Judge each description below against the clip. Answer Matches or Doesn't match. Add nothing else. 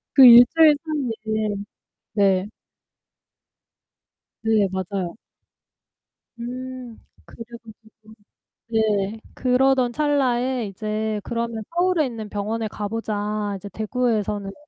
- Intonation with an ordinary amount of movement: Matches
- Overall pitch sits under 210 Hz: Doesn't match